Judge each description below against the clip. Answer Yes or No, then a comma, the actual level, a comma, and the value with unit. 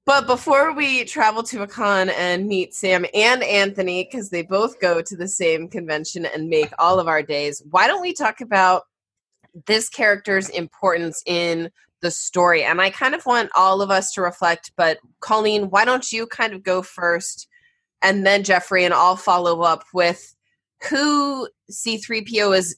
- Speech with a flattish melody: No, average, 4.3 semitones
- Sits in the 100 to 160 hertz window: No, high, 190 Hz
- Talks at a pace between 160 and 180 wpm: Yes, average, 175 wpm